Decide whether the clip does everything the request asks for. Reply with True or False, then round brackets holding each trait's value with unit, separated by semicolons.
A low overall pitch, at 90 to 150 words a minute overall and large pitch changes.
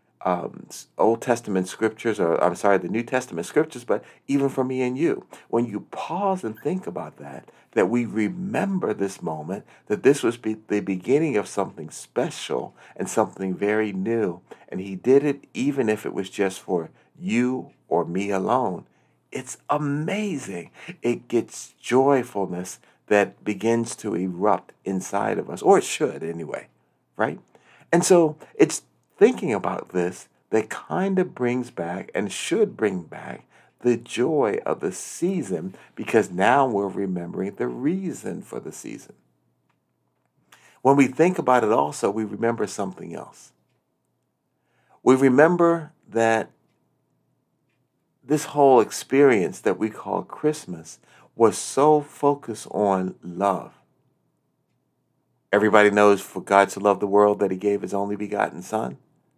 True (110 Hz; 145 wpm; 5.8 semitones)